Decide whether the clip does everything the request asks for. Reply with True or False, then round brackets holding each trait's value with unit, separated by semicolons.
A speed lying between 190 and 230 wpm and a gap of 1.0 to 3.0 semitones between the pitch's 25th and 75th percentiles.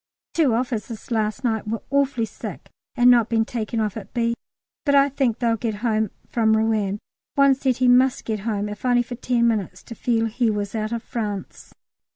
True (195 wpm; 2.4 semitones)